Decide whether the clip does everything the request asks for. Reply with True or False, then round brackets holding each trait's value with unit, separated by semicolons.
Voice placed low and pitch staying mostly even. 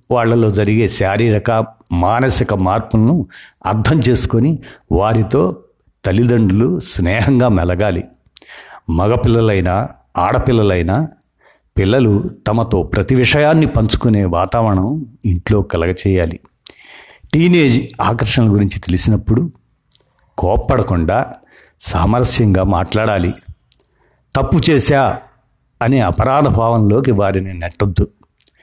False (110 Hz; 4.0 semitones)